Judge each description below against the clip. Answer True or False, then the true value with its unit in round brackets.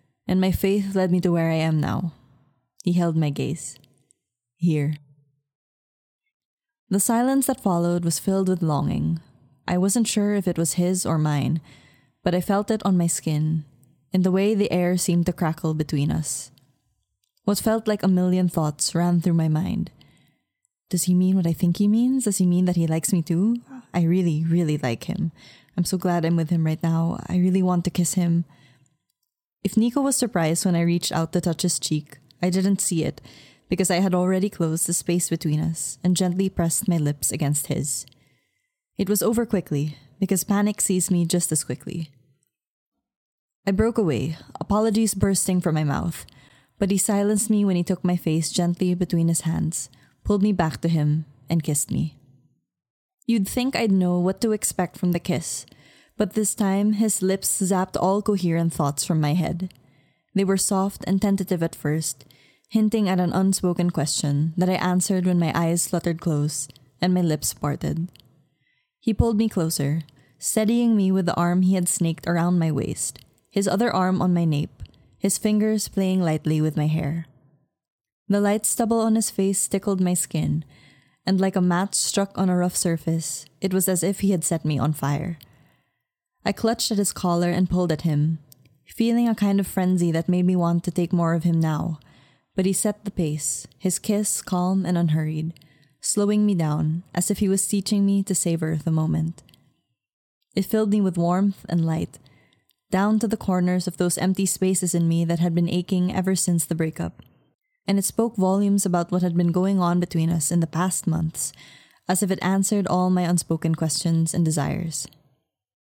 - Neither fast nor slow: True (190 wpm)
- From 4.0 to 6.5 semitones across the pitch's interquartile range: False (3.6 semitones)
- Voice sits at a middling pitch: True (175 Hz)